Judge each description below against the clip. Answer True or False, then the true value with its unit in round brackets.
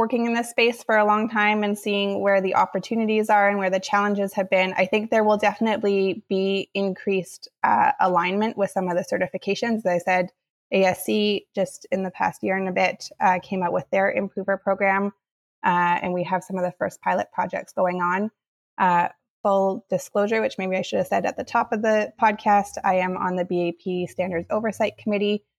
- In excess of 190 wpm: True (205 wpm)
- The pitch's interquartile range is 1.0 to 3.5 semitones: True (2.4 semitones)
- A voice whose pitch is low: False (195 Hz)